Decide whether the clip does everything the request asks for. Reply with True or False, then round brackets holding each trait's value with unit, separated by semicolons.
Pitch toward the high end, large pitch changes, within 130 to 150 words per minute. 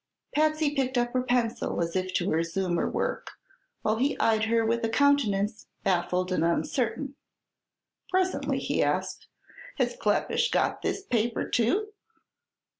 True (230 Hz; 6.5 semitones; 140 wpm)